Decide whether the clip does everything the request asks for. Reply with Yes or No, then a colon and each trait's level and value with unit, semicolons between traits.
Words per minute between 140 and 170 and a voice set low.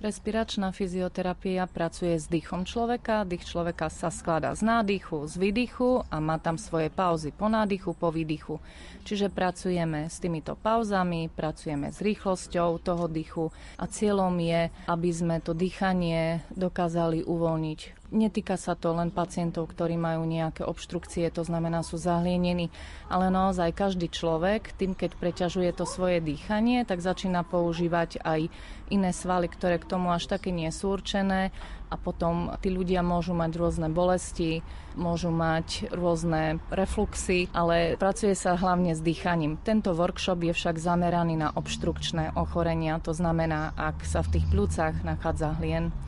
No: average, 150 wpm; medium, 175 Hz